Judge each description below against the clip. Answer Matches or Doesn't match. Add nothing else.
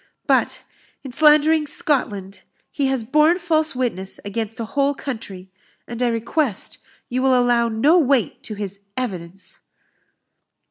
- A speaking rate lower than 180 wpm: Matches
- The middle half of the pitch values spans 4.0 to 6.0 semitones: Matches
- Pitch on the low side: Doesn't match